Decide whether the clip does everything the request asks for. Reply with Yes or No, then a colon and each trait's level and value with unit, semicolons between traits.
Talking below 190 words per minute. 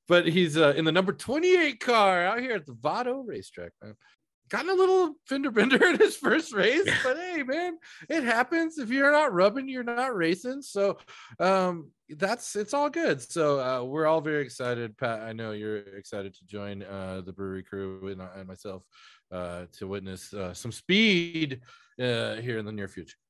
No: average, 195 wpm